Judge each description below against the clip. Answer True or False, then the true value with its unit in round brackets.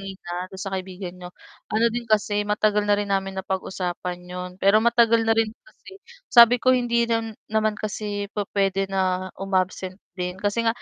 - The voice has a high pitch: True (200 Hz)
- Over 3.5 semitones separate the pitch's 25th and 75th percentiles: False (2.7 semitones)